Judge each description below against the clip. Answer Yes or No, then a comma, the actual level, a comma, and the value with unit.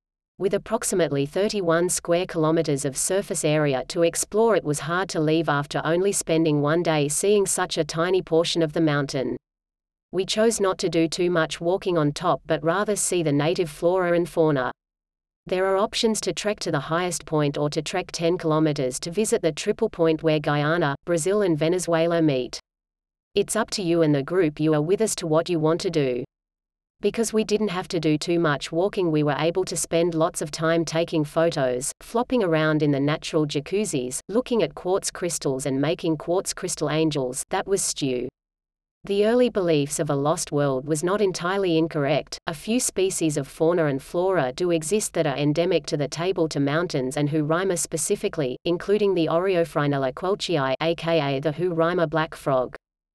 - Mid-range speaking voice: Yes, medium, 165 Hz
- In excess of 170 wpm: Yes, average, 185 wpm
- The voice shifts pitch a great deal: No, average, 3.5 semitones